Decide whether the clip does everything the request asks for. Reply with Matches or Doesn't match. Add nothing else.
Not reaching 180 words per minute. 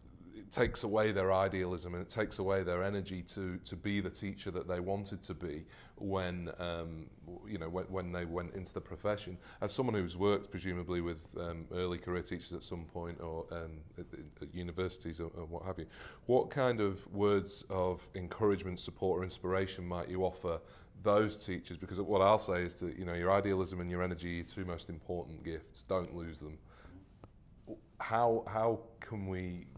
Doesn't match